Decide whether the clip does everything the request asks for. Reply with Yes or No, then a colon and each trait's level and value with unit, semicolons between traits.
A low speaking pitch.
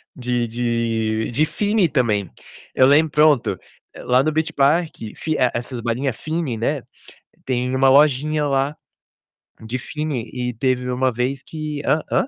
Yes: low, 130 Hz